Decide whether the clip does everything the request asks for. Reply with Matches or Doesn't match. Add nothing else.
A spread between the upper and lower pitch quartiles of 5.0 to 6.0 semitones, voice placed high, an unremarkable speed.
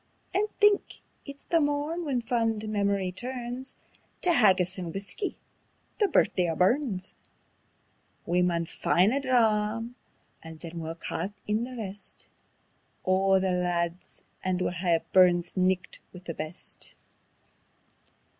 Doesn't match